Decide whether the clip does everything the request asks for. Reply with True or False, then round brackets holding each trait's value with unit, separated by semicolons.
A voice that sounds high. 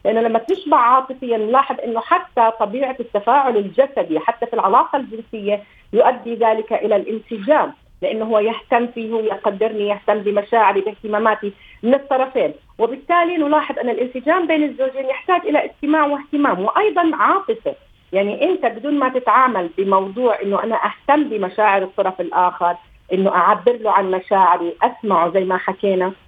True (230 Hz)